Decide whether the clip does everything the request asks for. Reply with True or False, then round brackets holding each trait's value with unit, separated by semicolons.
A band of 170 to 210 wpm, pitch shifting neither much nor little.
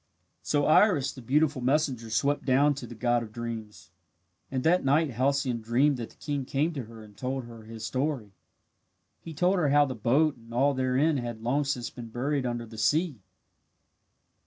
True (185 wpm; 3.7 semitones)